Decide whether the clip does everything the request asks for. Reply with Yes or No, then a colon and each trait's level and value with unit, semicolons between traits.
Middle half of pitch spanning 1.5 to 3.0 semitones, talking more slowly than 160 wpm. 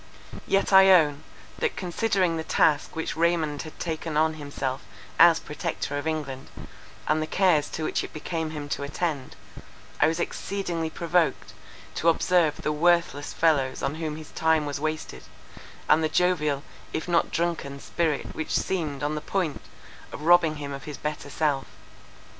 No: narrow, 2.5 semitones; average, 165 wpm